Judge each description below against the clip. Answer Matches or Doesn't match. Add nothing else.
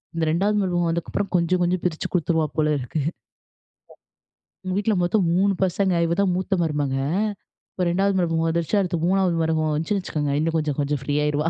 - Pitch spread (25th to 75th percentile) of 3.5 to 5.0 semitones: Doesn't match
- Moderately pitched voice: Matches